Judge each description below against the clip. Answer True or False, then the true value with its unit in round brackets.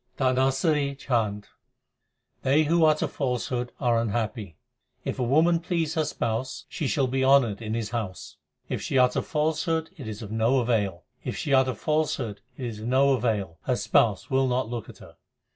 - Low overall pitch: True (130 Hz)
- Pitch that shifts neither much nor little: True (3.7 semitones)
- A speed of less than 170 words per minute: False (175 wpm)